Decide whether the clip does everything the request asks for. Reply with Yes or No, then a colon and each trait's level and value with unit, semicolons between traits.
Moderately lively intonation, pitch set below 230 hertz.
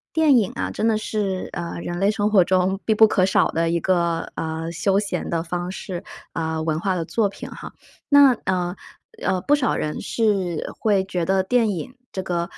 Yes: average, 3.7 semitones; medium, 185 Hz